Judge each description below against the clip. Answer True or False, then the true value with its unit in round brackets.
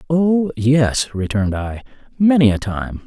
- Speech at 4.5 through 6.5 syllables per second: False (4.1 syllables/s)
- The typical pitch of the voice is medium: False (125 Hz)